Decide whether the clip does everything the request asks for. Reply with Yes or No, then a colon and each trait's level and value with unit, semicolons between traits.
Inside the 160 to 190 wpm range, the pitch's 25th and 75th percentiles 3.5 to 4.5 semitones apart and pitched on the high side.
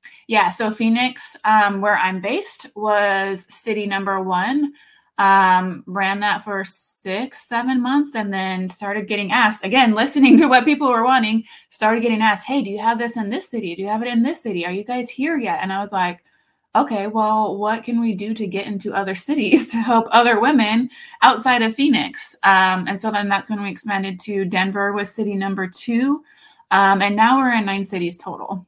No: fast, 205 wpm; average, 4.0 semitones; high, 215 Hz